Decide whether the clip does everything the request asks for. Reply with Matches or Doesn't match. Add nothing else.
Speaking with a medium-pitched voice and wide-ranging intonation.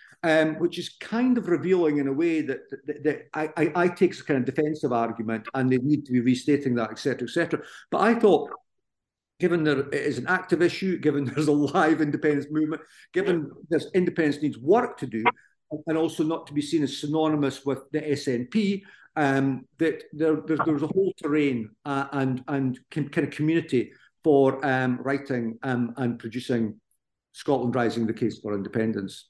Doesn't match